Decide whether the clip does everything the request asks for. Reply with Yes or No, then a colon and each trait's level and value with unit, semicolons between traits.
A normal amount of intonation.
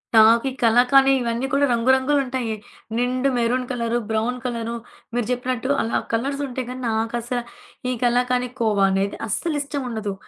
No: narrow, 2.0 semitones